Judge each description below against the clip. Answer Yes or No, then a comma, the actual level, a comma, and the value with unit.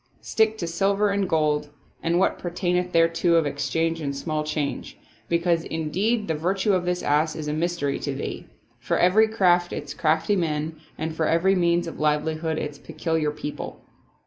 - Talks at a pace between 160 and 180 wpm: Yes, average, 170 wpm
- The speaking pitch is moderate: Yes, medium, 165 Hz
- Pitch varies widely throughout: No, average, 2.7 semitones